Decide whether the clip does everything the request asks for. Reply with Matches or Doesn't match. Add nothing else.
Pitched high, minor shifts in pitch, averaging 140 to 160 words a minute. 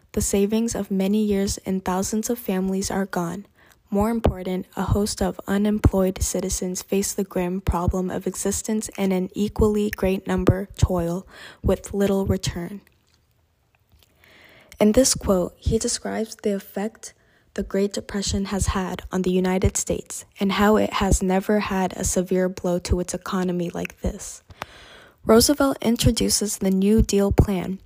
Matches